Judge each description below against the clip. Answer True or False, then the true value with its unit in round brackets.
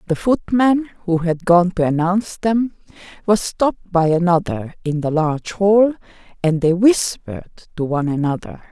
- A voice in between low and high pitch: True (180 Hz)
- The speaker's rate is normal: True (150 wpm)